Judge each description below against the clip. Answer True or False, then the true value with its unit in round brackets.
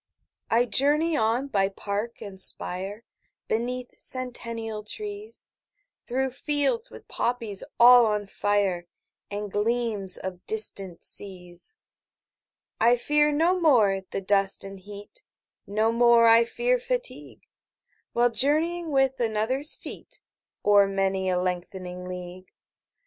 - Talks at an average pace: False (120 wpm)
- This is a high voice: True (225 Hz)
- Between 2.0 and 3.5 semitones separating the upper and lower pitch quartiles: False (5.2 semitones)